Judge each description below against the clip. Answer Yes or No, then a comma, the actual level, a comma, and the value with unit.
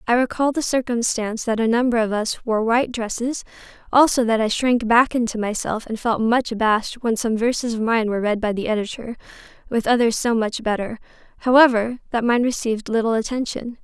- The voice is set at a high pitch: Yes, high, 230 Hz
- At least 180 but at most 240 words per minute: Yes, average, 185 wpm